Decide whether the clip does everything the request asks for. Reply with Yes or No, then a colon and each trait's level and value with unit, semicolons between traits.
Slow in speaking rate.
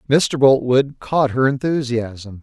Yes: slow, 125 wpm